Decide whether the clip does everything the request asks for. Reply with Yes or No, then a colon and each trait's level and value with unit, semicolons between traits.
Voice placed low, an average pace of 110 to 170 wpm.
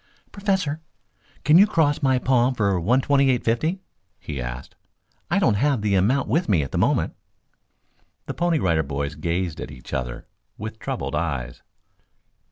Yes: low, 115 Hz; average, 165 wpm